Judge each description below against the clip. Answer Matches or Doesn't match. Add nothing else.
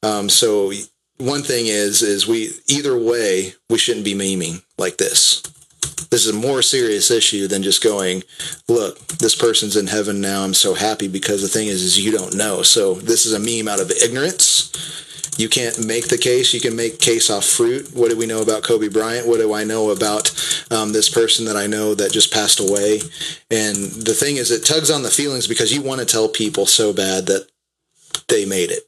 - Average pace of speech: Doesn't match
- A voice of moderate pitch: Doesn't match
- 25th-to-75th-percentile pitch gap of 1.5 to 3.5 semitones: Matches